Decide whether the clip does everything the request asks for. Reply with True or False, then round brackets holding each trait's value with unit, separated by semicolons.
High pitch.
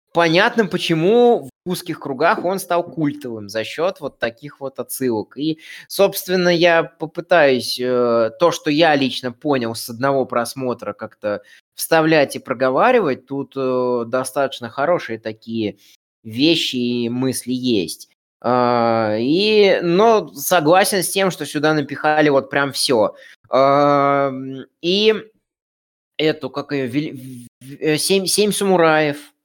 False (140 Hz)